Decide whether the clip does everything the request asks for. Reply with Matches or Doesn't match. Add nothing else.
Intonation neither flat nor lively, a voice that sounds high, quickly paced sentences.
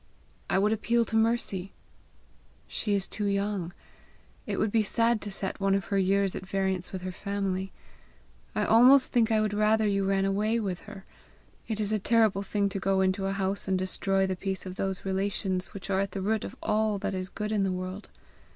Doesn't match